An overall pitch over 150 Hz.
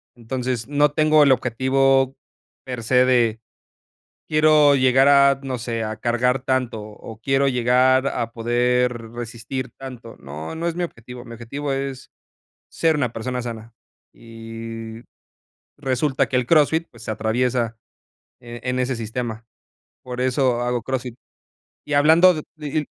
No: low, 125 Hz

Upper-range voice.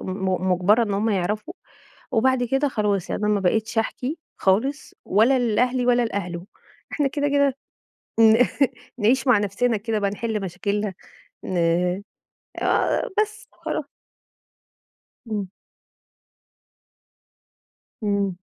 Yes: high, 220 Hz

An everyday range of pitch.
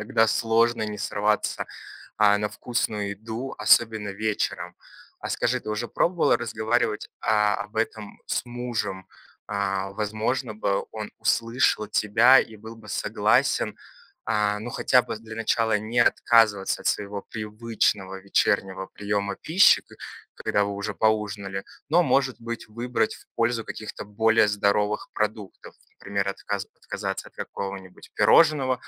No: narrow, 2.1 semitones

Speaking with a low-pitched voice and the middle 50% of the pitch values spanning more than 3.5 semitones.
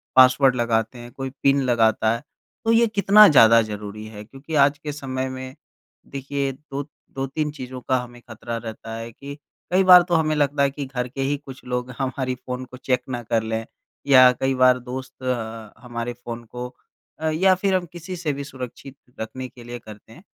No: low, 130 Hz; average, 2.9 semitones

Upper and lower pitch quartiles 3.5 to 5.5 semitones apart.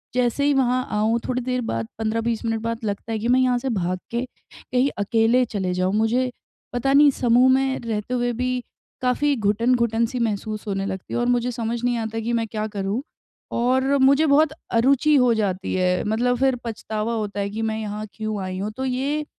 No: average, 2.9 semitones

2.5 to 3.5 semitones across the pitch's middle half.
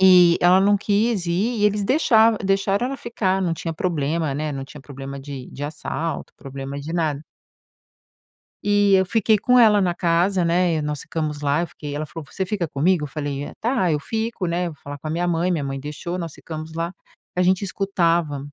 No: average, 4.7 semitones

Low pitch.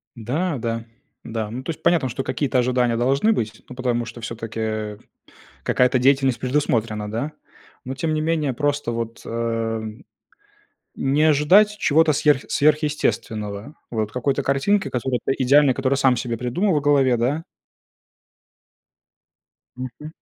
Yes: low, 130 Hz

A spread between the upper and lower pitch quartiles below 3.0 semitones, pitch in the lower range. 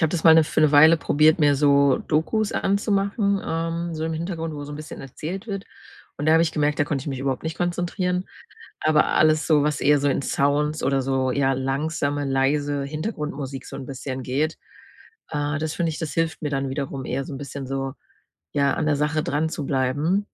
No: narrow, 2.6 semitones; medium, 150 Hz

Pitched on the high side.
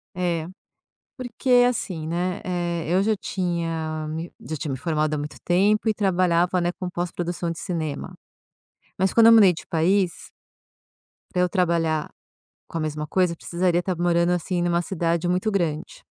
No: medium, 175 Hz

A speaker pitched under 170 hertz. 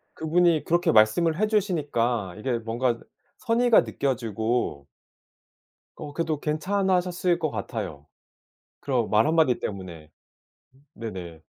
Yes: low, 135 Hz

